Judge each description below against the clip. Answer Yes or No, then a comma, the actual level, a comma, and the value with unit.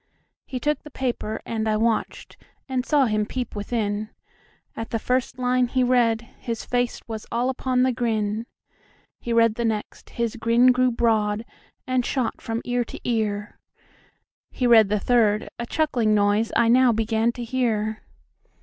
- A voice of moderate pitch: No, high, 235 Hz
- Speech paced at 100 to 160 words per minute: Yes, average, 140 wpm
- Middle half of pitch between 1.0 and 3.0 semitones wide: Yes, narrow, 2.4 semitones